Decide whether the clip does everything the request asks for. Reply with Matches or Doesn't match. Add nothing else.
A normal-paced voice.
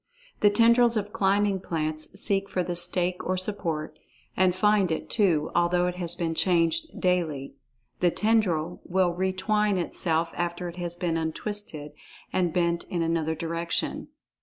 Matches